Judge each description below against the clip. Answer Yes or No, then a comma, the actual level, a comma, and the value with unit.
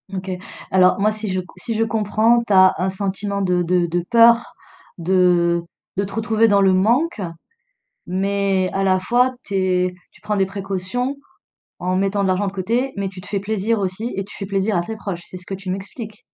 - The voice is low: No, high, 195 Hz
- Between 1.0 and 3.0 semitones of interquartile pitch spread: Yes, narrow, 2.5 semitones